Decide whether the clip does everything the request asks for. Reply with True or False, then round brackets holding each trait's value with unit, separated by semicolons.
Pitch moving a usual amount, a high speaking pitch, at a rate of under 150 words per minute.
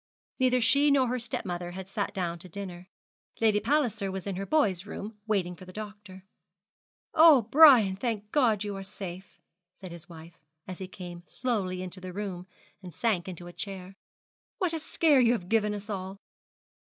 False (3.8 semitones; 200 Hz; 180 wpm)